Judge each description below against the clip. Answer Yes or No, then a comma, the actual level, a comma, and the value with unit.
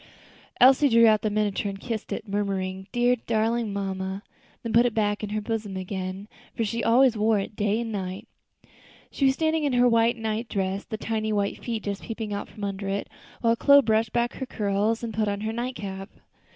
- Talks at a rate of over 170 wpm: Yes, fast, 205 wpm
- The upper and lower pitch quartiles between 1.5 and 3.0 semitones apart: Yes, narrow, 2.5 semitones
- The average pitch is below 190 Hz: No, high, 215 Hz